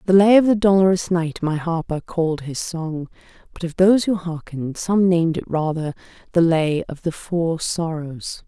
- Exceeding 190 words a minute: No, average, 185 wpm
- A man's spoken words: No, female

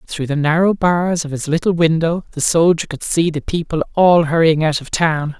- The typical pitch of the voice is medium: Yes, medium, 160 Hz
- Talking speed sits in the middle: No, fast, 210 wpm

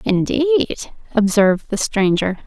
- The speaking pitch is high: Yes, high, 220 Hz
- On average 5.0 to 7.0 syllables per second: No, 4.2 syllables/s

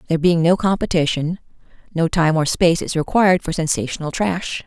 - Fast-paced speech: No, average, 165 wpm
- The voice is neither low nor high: Yes, medium, 170 Hz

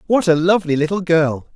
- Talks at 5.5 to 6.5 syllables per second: Yes, 5.8 syllables/s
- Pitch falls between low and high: Yes, medium, 170 Hz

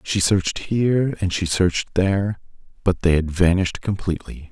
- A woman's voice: No, male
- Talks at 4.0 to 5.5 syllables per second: Yes, 5.4 syllables/s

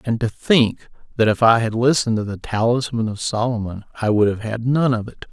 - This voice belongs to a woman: No, male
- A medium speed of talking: No, fast, 225 wpm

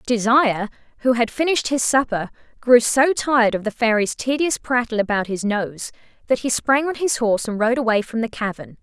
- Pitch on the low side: No, high, 235 Hz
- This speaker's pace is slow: No, average, 195 wpm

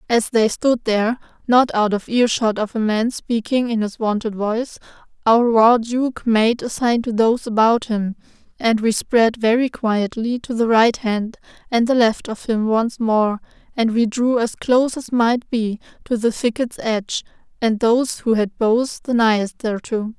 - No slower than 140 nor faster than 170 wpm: No, average, 185 wpm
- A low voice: No, high, 230 Hz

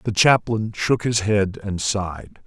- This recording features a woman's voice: No, male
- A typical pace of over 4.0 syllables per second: No, 3.9 syllables/s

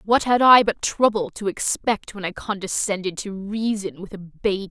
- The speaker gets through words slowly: No, average, 190 wpm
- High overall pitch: Yes, high, 200 Hz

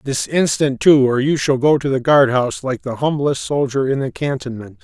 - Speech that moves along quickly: Yes, fast, 225 wpm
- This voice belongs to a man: Yes, male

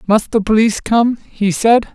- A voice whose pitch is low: No, high, 215 Hz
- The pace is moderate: Yes, average, 185 wpm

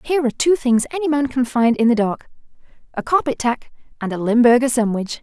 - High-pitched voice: Yes, very high, 250 Hz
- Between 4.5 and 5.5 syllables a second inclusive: No, 6.1 syllables/s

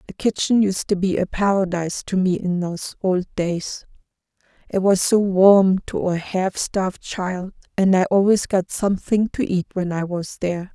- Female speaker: Yes, female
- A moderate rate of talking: Yes, average, 180 wpm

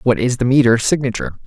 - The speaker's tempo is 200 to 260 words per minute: Yes, fast, 205 wpm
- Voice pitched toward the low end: Yes, low, 125 Hz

